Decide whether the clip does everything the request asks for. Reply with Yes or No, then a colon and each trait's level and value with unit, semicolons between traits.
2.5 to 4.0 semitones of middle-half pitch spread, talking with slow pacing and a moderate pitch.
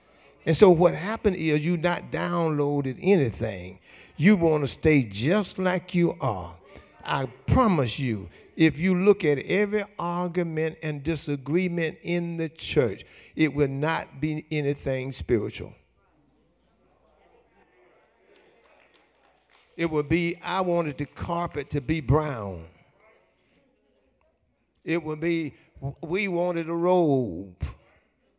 Yes: average, 3.4 semitones; slow, 115 wpm; medium, 160 Hz